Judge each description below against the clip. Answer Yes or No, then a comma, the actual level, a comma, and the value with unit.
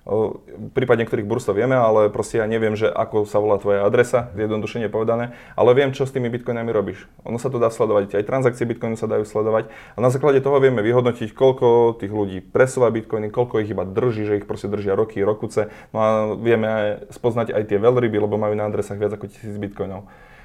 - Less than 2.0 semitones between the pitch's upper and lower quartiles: No, narrow, 2.4 semitones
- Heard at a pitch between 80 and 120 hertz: Yes, low, 110 Hz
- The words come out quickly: Yes, fast, 210 wpm